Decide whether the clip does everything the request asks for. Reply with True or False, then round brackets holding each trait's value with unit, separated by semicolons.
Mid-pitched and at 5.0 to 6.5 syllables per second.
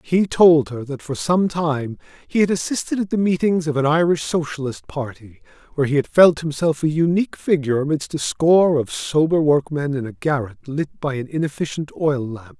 True (150 Hz; 5.3 syllables/s)